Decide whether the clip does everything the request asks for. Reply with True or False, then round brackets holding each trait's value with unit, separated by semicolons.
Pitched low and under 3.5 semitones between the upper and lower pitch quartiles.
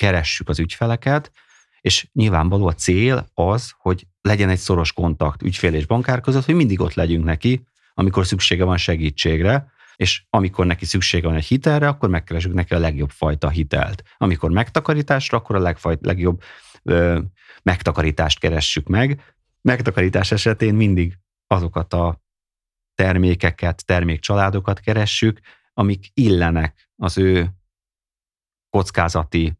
False (90 Hz; 3.8 semitones)